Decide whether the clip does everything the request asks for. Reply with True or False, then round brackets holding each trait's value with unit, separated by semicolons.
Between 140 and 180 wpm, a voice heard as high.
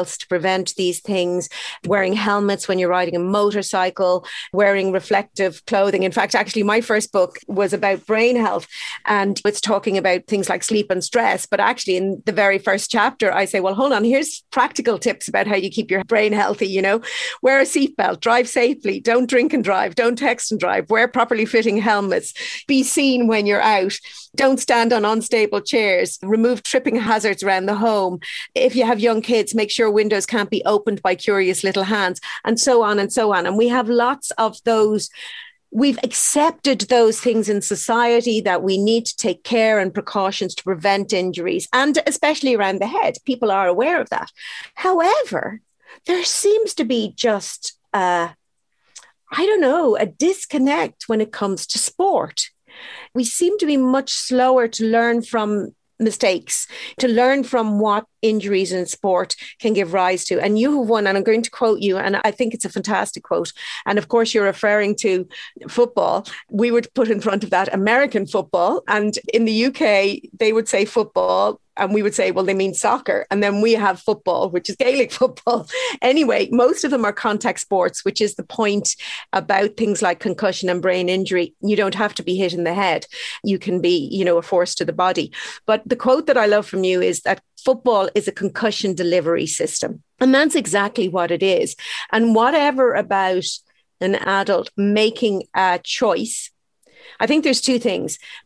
False (190 wpm; 215 Hz)